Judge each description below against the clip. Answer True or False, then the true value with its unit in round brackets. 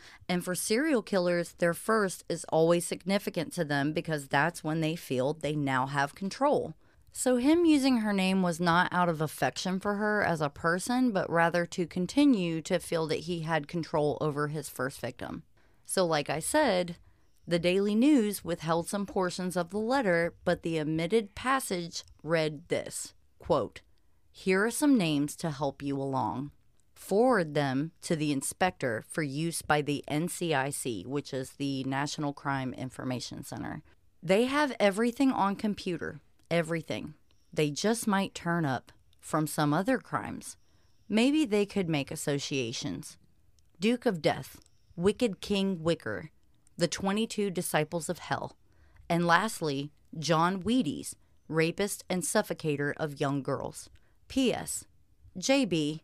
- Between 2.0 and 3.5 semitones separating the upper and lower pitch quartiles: False (5.1 semitones)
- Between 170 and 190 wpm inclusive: False (145 wpm)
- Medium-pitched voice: True (170 Hz)